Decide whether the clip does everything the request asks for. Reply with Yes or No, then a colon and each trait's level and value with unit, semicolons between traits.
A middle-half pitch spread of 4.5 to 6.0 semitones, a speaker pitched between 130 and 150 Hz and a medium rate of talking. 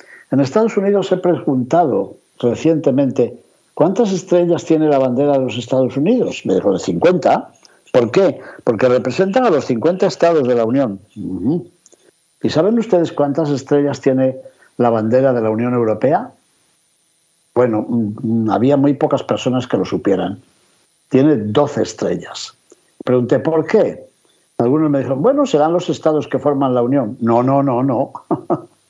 Yes: average, 5.0 semitones; medium, 140 Hz; average, 145 wpm